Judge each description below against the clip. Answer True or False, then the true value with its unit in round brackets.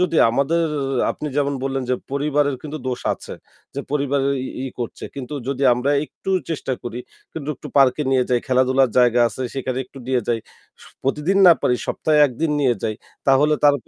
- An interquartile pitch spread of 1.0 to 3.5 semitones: True (2.6 semitones)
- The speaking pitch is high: False (135 Hz)